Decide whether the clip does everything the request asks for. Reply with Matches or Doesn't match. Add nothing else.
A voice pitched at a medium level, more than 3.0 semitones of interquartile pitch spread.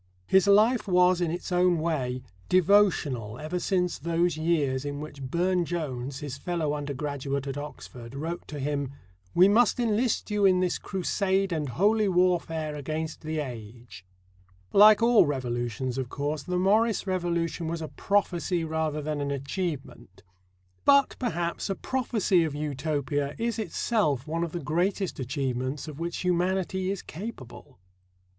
Matches